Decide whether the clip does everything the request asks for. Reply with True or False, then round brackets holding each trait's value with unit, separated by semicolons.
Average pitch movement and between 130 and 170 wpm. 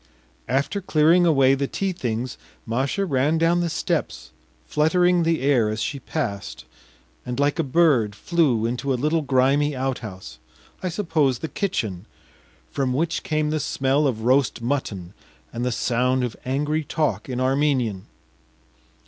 True (4.2 semitones; 150 wpm)